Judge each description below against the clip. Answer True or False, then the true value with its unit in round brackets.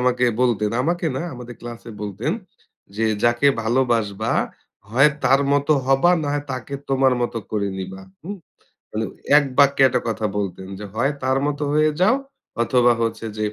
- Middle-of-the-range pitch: False (125 Hz)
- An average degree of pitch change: True (4.0 semitones)